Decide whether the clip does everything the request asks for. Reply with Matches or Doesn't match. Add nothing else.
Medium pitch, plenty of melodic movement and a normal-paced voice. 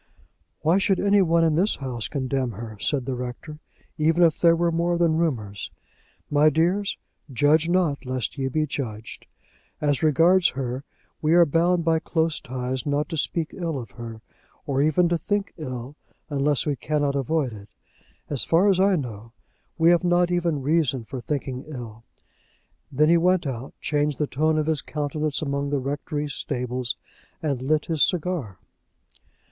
Doesn't match